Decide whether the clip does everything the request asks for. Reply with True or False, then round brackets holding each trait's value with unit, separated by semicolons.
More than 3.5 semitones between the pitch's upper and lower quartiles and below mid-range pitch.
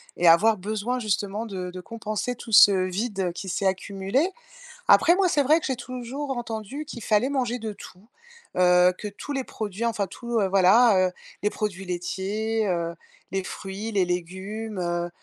False (4.1 semitones; 210 Hz)